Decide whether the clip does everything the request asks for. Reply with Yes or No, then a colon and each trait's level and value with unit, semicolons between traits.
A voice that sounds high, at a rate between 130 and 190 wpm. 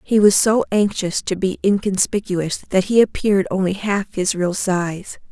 Yes: high, 195 Hz; average, 170 wpm